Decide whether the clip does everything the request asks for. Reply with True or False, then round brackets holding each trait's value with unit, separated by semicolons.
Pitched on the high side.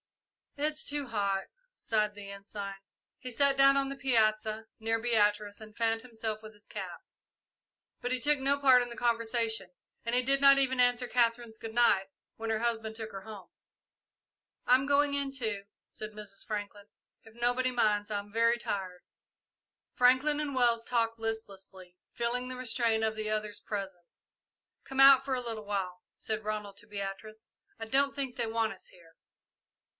True (225 Hz)